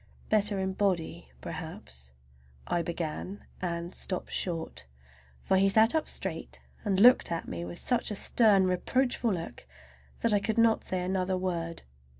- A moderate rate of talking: Yes, average, 150 wpm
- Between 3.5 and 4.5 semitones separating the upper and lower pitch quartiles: Yes, average, 3.9 semitones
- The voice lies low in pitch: No, medium, 185 Hz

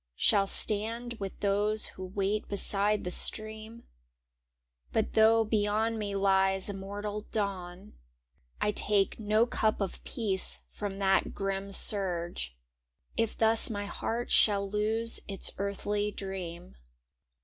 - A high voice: Yes, high, 205 Hz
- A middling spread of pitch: No, narrow, 1.9 semitones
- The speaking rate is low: Yes, slow, 125 wpm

